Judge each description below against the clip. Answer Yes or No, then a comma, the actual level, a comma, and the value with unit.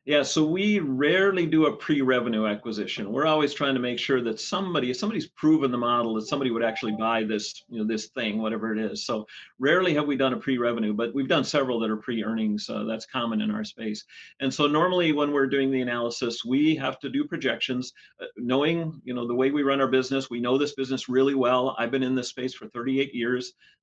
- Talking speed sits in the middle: No, fast, 230 wpm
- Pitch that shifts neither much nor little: Yes, average, 3.6 semitones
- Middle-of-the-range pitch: No, low, 130 Hz